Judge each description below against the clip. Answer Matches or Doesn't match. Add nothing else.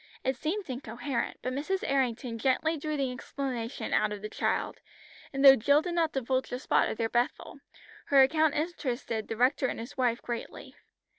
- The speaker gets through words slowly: Doesn't match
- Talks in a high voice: Matches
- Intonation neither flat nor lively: Matches